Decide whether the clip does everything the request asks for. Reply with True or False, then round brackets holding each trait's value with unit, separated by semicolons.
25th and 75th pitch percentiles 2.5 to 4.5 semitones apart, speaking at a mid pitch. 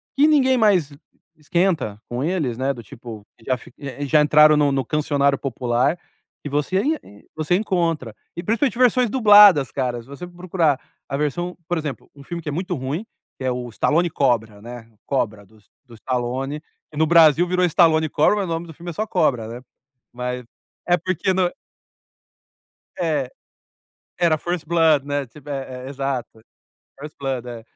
False (5.5 semitones; 150 Hz)